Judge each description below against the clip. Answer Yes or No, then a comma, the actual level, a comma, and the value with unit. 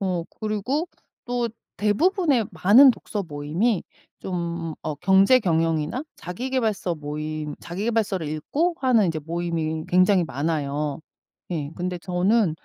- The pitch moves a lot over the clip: Yes, wide, 5.8 semitones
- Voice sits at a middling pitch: Yes, medium, 180 Hz